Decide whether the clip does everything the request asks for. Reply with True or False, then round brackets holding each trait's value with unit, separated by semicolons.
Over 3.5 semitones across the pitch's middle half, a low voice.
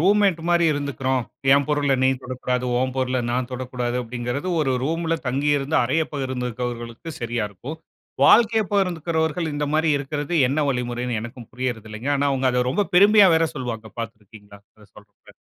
True (4.5 semitones; 130 Hz)